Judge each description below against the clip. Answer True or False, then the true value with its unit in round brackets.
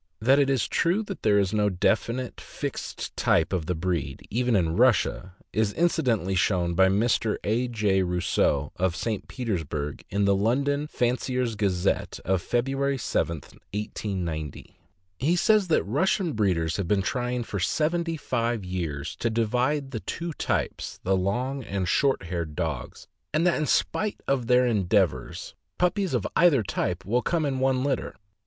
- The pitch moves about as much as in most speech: False (6.3 semitones)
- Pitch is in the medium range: False (110 Hz)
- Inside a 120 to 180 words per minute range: True (160 wpm)